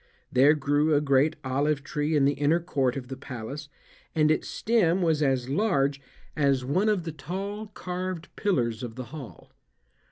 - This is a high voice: No, medium, 150 Hz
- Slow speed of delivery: No, average, 170 wpm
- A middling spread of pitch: Yes, average, 3.9 semitones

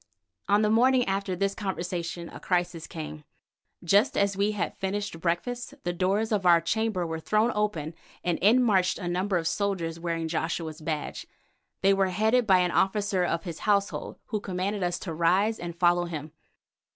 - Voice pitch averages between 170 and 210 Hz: Yes, medium, 185 Hz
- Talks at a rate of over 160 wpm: Yes, average, 175 wpm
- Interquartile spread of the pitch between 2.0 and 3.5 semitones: Yes, average, 3.2 semitones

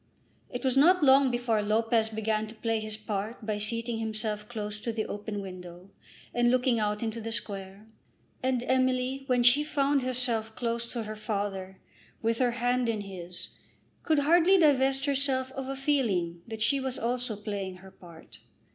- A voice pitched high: Yes, high, 230 Hz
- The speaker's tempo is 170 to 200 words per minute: Yes, average, 175 wpm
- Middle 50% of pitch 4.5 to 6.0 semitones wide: No, average, 3.6 semitones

